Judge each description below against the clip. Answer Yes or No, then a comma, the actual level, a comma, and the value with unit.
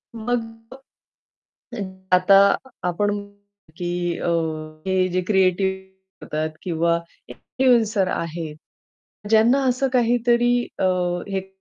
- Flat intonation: No, average, 4.6 semitones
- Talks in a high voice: Yes, high, 195 Hz